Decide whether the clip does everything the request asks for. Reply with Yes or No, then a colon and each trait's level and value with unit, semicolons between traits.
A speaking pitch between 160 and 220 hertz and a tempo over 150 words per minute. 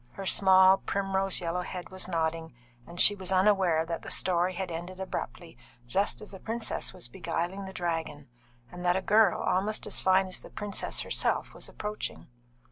Yes: medium, 185 Hz; average, 180 wpm